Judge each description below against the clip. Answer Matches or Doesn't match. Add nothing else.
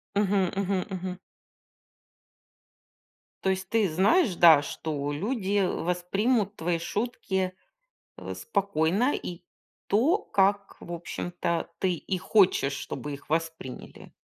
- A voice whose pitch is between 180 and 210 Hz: Matches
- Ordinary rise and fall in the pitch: Matches